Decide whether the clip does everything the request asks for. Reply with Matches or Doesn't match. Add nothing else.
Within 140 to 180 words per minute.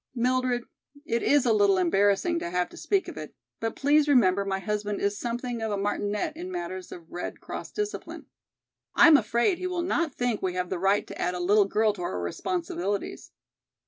Doesn't match